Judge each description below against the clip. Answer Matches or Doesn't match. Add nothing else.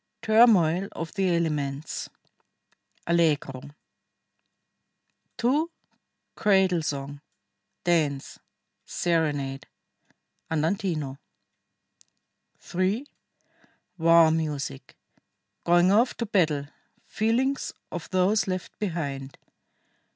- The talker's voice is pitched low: Doesn't match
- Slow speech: Matches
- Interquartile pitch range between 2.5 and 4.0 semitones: Doesn't match